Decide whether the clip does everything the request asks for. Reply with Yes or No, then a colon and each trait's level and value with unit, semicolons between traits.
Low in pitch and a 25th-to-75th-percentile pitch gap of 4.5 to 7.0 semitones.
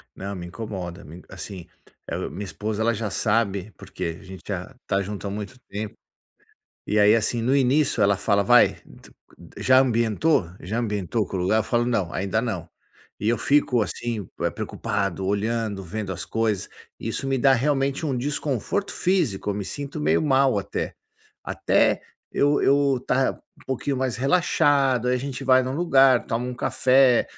Yes: low, 115 Hz; average, 4.8 semitones